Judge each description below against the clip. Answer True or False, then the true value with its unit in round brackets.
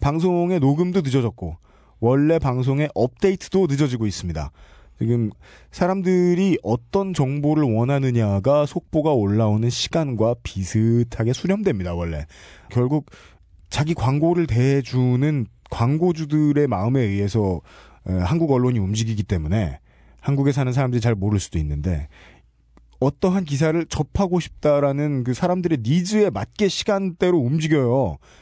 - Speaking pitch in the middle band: False (130 Hz)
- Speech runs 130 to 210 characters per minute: False (310 characters per minute)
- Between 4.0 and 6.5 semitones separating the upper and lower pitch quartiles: False (7.7 semitones)